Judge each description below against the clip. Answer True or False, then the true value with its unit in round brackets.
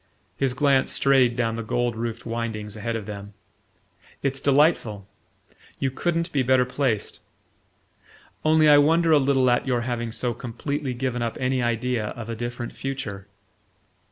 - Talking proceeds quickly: False (155 wpm)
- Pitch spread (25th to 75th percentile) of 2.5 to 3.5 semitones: True (2.9 semitones)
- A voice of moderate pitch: False (125 Hz)